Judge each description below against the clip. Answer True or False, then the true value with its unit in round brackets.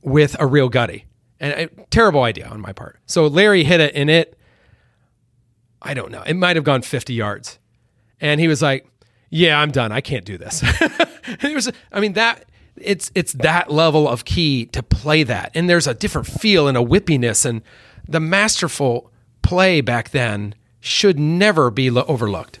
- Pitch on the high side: False (140 Hz)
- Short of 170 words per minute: False (190 wpm)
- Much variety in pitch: True (5.8 semitones)